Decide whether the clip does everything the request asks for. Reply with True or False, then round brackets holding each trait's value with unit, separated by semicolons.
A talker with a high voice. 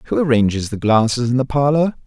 False (125 Hz)